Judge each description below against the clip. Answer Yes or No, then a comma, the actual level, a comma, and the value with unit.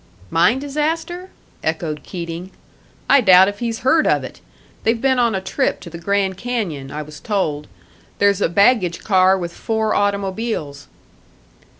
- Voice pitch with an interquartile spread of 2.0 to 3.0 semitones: No, wide, 5.4 semitones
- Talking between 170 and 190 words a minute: No, average, 155 wpm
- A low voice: No, high, 200 Hz